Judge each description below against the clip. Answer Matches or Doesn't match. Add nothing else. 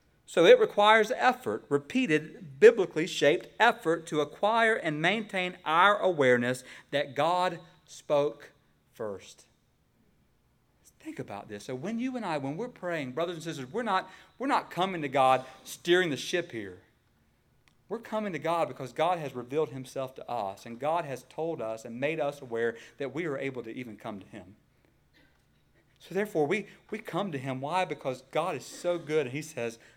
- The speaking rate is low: Doesn't match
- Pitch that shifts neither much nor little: Doesn't match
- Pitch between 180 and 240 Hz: Doesn't match